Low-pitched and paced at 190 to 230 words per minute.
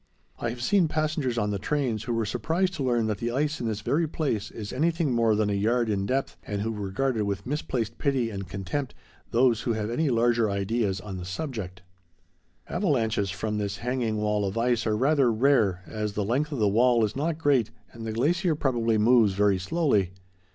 Yes: low, 115 Hz; fast, 205 wpm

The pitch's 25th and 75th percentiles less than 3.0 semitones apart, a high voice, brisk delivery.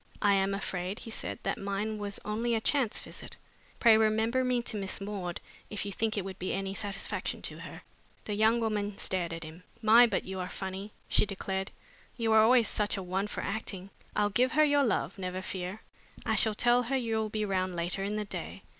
Yes: narrow, 2.6 semitones; high, 205 Hz; fast, 215 wpm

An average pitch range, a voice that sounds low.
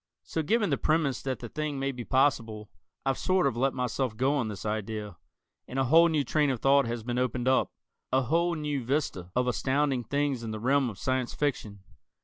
Yes: average, 3.6 semitones; low, 130 Hz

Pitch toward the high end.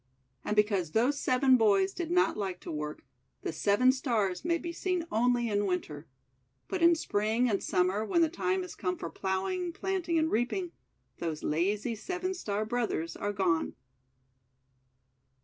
Yes: high, 220 Hz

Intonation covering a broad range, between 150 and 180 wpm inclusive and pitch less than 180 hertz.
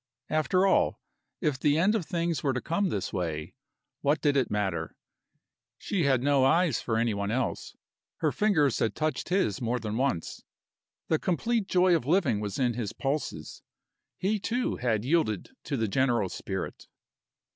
Yes: wide, 7.3 semitones; average, 165 wpm; low, 135 Hz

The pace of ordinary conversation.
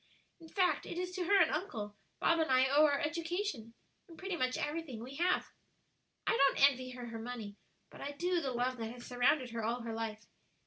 No: fast, 215 wpm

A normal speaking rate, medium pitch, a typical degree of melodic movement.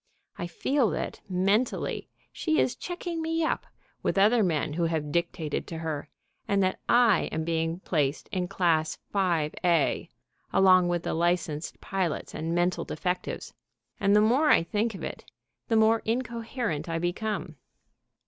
Yes: average, 150 wpm; medium, 180 Hz; average, 5.0 semitones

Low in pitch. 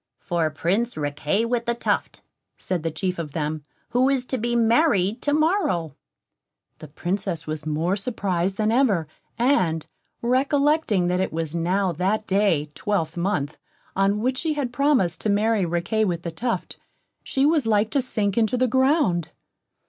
No: high, 200 Hz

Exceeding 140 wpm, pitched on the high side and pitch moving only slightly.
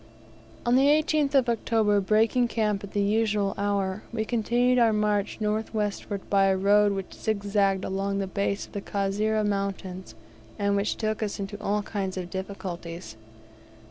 Yes: average, 170 wpm; high, 205 Hz; narrow, 1.8 semitones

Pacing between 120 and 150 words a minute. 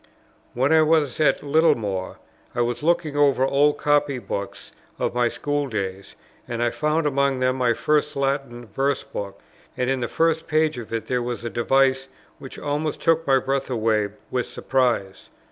No: average, 175 wpm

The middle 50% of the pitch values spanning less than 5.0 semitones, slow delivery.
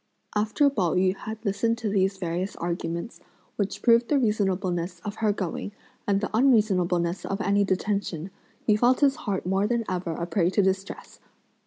No: average, 3.1 semitones; average, 170 wpm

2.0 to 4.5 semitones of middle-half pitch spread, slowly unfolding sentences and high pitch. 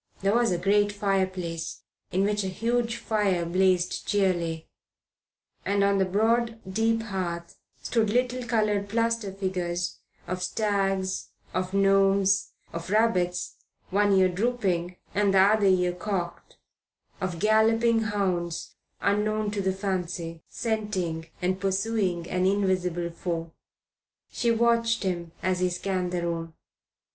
Yes: average, 2.9 semitones; slow, 125 wpm; high, 195 Hz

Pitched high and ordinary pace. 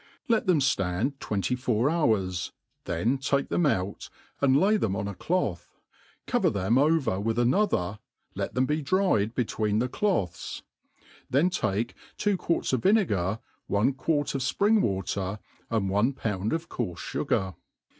No: low, 120 Hz; average, 155 wpm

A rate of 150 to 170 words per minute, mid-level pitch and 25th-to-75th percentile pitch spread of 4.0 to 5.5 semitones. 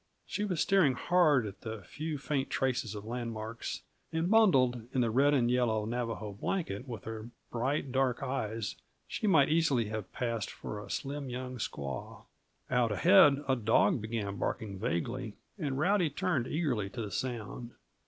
No: average, 165 wpm; low, 125 Hz; average, 4.6 semitones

